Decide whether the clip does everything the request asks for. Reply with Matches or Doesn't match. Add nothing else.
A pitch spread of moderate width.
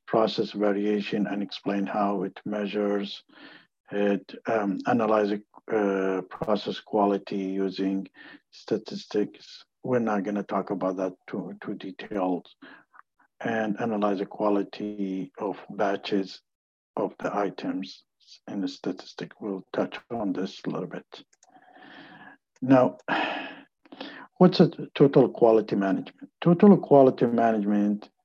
Doesn't match